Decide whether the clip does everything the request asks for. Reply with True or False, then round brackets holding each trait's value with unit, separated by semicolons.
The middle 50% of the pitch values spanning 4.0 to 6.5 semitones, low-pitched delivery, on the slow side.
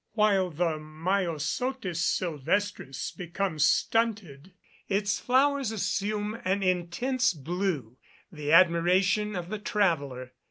False (4.5 semitones; 185 Hz; 95 wpm)